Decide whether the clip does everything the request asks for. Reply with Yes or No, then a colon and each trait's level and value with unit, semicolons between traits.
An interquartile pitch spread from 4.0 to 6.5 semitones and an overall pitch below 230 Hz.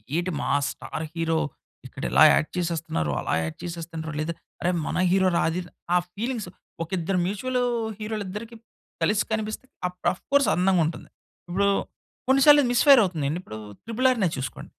Yes: average, 5.0 semitones; medium, 185 Hz